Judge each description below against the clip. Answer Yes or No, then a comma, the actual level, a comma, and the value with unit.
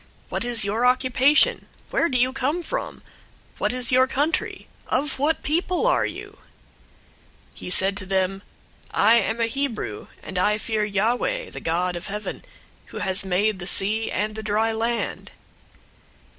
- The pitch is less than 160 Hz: No, high, 225 Hz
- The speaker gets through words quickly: No, average, 160 wpm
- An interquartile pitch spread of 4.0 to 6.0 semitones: Yes, average, 4.6 semitones